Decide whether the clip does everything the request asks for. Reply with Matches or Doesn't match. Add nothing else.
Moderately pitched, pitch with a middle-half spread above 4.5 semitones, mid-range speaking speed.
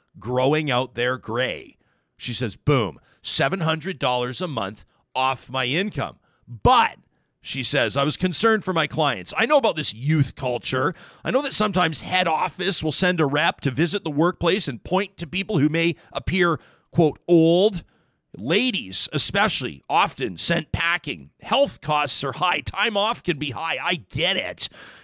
Matches